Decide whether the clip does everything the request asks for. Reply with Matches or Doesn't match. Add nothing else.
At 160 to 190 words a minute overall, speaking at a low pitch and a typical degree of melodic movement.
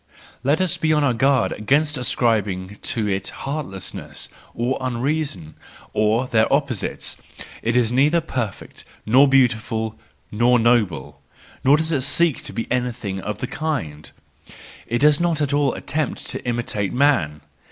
Doesn't match